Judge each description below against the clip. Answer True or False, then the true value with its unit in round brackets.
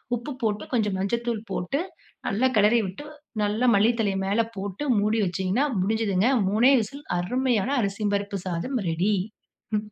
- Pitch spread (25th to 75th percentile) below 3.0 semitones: False (3.3 semitones)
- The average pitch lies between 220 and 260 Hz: False (210 Hz)